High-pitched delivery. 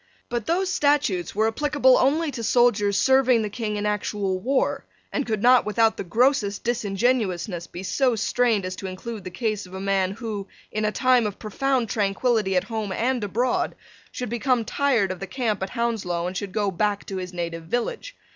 Yes: high, 215 Hz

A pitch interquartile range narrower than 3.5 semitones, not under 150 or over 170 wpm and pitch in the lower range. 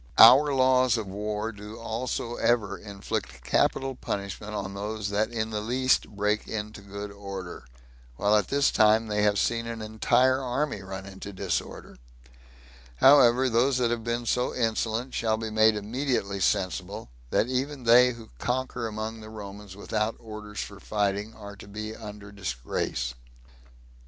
Yes: average, 2.7 semitones; average, 155 wpm; low, 110 Hz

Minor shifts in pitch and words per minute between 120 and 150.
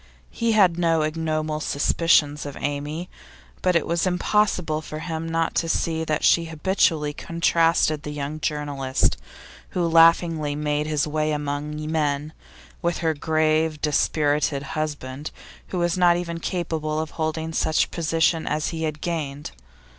Yes: narrow, 1.9 semitones; average, 145 wpm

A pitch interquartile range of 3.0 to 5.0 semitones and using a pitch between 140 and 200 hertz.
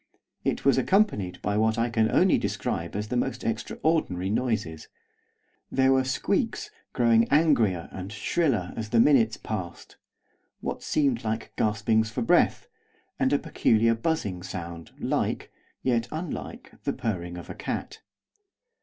No: average, 4.6 semitones; low, 115 Hz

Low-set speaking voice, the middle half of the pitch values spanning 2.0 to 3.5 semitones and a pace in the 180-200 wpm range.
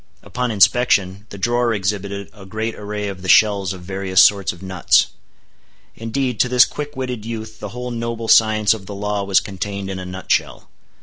Yes: low, 105 Hz; average, 3.0 semitones; average, 190 wpm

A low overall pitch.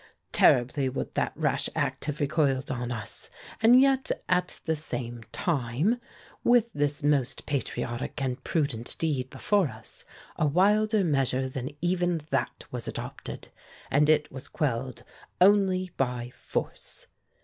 No: medium, 145 Hz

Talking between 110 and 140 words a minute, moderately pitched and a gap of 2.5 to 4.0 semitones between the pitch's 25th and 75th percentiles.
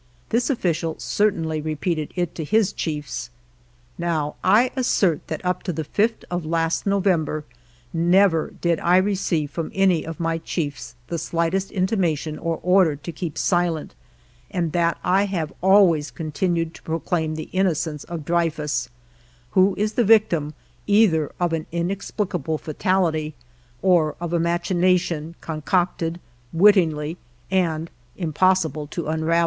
Yes: slow, 135 wpm; medium, 170 Hz; average, 2.9 semitones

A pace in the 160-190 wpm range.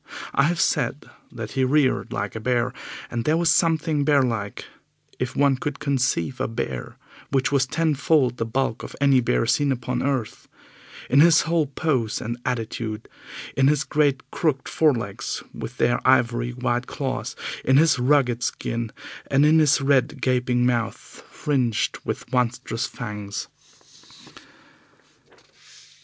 No: average, 145 wpm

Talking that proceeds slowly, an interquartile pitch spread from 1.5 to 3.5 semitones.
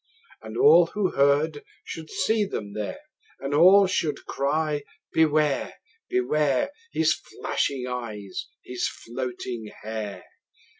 No: slow, 110 wpm; average, 4.6 semitones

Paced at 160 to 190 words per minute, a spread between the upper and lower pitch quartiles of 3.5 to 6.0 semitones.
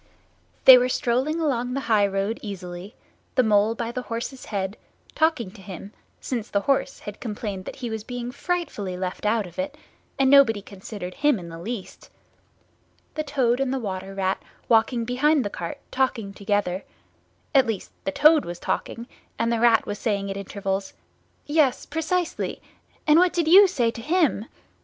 Yes: average, 165 wpm; wide, 5.4 semitones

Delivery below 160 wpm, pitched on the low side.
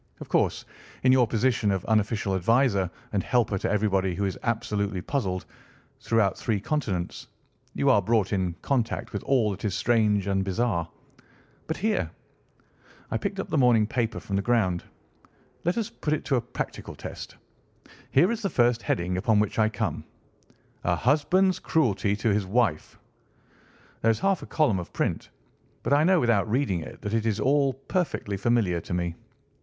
No: average, 170 wpm; low, 110 Hz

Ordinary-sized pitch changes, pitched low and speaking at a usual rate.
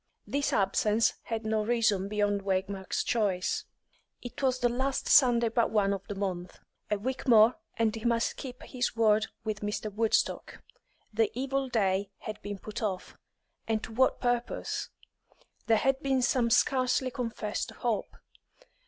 No: average, 3.1 semitones; high, 225 Hz; average, 155 wpm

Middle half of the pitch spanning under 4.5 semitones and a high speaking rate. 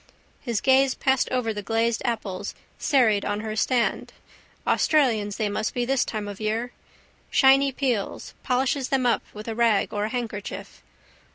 No: average, 3.5 semitones; average, 160 wpm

